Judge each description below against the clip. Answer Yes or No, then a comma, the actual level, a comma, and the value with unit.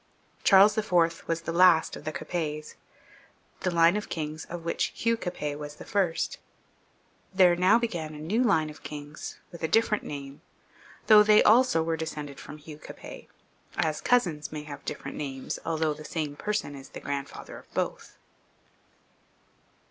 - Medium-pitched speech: Yes, medium, 160 Hz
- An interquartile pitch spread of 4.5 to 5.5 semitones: No, average, 3.8 semitones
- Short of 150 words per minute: No, average, 165 wpm